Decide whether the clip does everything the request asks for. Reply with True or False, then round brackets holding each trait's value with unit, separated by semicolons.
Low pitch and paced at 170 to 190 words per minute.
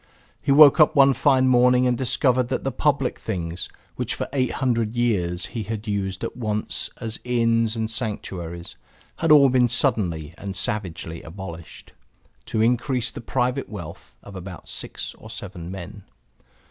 False (115 Hz; 160 wpm)